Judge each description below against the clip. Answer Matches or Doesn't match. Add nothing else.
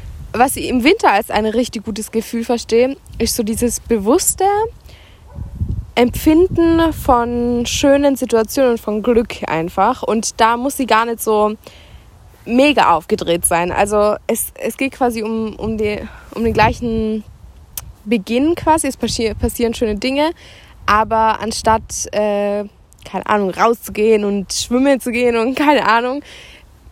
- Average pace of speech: Matches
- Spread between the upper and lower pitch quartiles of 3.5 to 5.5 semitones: Doesn't match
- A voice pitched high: Matches